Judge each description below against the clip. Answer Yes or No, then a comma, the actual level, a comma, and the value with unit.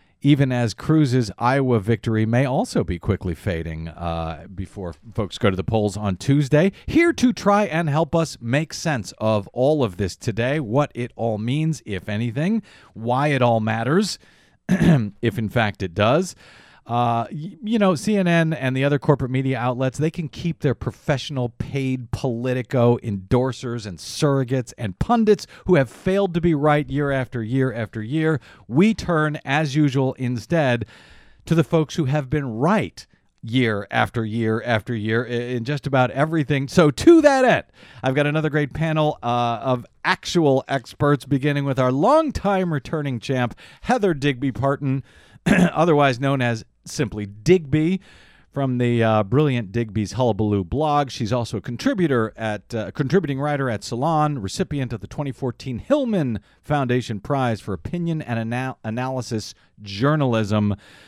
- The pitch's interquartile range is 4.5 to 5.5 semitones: Yes, average, 5.1 semitones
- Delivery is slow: No, average, 155 wpm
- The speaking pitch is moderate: No, low, 130 Hz